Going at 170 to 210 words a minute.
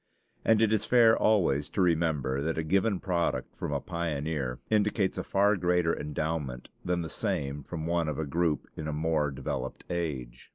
Yes: average, 180 wpm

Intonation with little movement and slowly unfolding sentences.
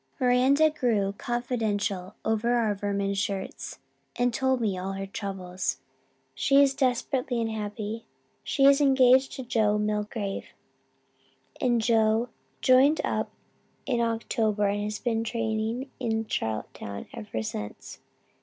No: average, 3.5 semitones; slow, 120 wpm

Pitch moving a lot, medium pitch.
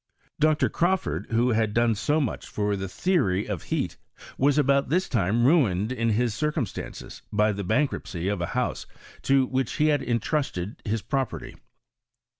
No: wide, 5.7 semitones; low, 115 Hz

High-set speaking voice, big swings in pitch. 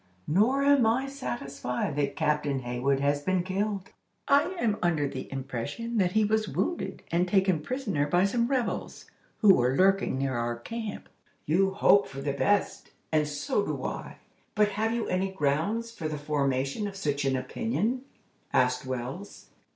No: medium, 180 Hz; wide, 7.5 semitones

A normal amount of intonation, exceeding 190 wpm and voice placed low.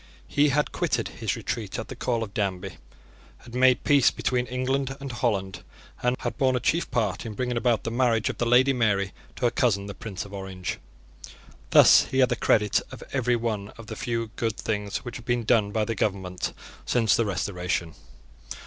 Yes: average, 3.6 semitones; average, 200 wpm; low, 115 Hz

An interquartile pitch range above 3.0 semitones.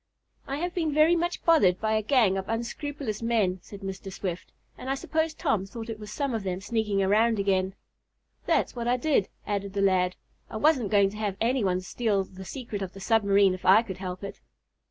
Yes: average, 3.9 semitones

